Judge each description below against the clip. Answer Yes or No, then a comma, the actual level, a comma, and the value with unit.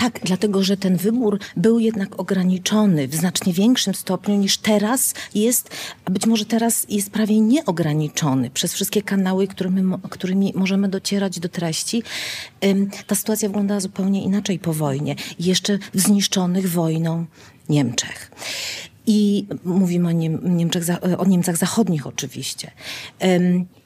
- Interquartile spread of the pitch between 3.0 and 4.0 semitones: No, narrow, 2.6 semitones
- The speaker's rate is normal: Yes, average, 130 wpm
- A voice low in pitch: No, high, 190 Hz